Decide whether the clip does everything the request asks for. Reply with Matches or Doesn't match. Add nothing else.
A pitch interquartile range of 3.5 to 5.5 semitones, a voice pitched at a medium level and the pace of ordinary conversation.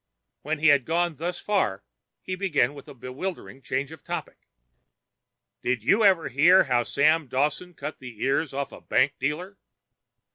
Matches